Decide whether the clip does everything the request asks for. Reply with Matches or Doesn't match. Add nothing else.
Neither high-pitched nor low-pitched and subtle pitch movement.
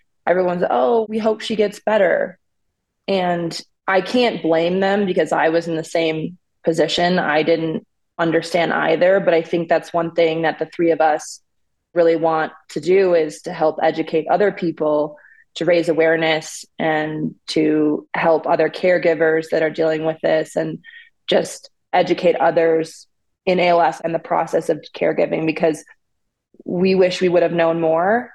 Matches